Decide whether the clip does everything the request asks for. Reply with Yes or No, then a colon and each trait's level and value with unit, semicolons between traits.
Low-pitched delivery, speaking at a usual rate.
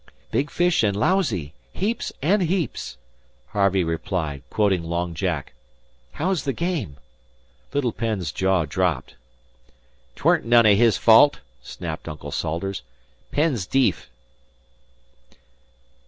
No: low, 100 Hz; slow, 110 wpm